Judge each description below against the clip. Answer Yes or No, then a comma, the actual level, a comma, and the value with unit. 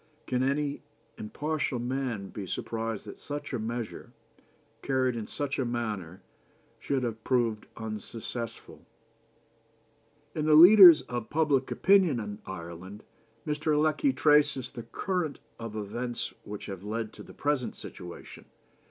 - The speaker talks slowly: Yes, slow, 130 wpm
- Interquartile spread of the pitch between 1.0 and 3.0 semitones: No, average, 5.2 semitones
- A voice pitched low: Yes, low, 120 Hz